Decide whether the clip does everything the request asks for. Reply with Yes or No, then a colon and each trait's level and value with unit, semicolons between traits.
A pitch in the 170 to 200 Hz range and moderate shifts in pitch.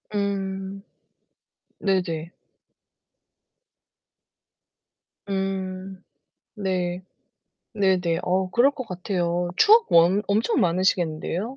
No: high, 190 Hz; narrow, 1.9 semitones